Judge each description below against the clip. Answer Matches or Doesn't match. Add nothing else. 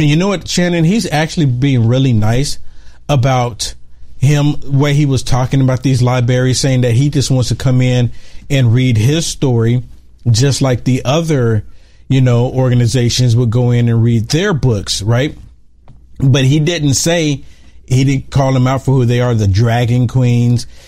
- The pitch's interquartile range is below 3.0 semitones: Matches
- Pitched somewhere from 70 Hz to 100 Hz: Doesn't match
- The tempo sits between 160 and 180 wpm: Matches